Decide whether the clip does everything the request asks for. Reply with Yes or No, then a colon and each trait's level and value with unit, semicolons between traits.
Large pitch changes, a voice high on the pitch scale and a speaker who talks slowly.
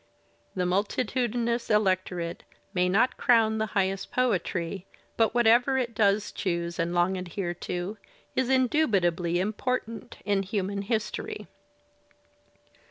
No: average, 4.5 semitones; high, 205 Hz; slow, 110 wpm